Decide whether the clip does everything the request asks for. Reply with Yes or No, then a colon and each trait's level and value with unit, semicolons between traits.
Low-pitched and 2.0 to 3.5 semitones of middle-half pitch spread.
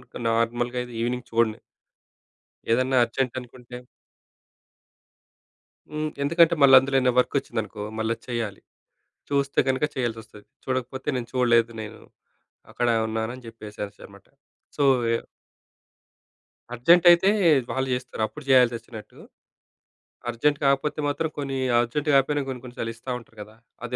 Yes: low, 125 Hz; average, 2.8 semitones